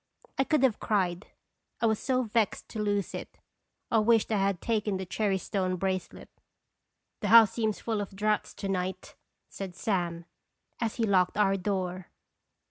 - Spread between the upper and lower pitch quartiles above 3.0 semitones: No, average, 2.7 semitones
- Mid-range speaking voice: No, high, 205 Hz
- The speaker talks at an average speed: Yes, average, 170 wpm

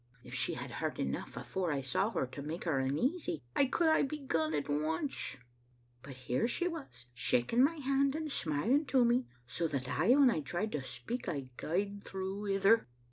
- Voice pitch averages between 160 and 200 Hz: Yes, high, 190 Hz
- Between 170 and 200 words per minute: Yes, average, 190 wpm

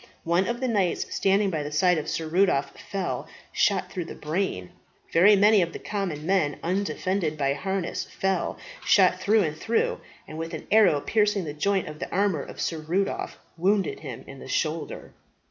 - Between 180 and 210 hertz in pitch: Yes, medium, 185 Hz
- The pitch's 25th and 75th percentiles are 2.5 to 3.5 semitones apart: No, average, 4.2 semitones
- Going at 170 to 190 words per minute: Yes, average, 180 wpm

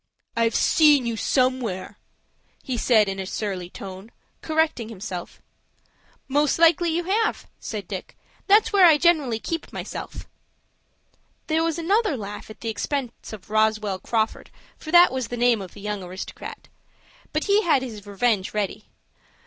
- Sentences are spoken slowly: No, average, 150 wpm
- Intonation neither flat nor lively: No, wide, 7.3 semitones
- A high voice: Yes, high, 235 Hz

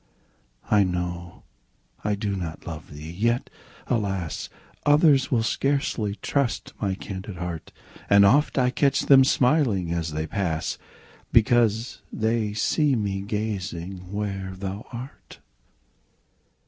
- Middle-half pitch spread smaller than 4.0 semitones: No, average, 4.6 semitones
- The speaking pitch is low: Yes, low, 100 Hz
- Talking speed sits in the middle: No, slow, 120 wpm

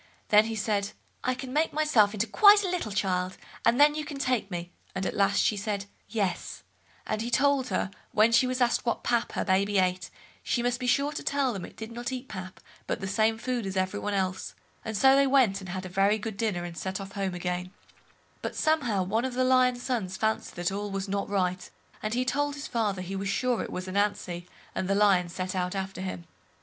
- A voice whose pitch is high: Yes, high, 210 Hz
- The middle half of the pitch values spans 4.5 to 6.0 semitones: Yes, average, 4.8 semitones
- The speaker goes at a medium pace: No, fast, 230 wpm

